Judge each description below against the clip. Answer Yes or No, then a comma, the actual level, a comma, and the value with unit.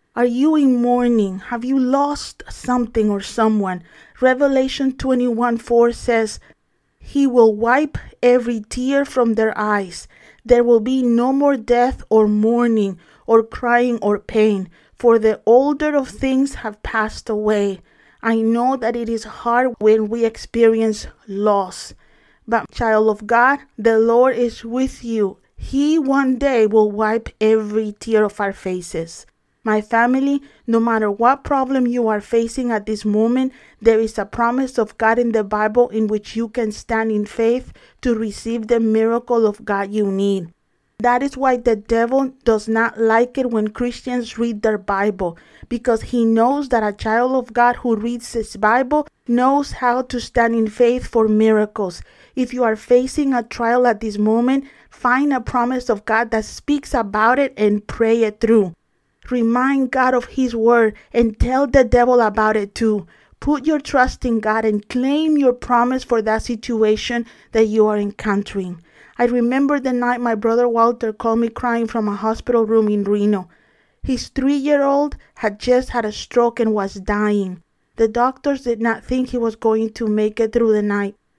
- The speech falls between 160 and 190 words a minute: Yes, average, 170 wpm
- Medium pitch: No, high, 230 Hz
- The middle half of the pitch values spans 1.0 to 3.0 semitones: Yes, narrow, 2.4 semitones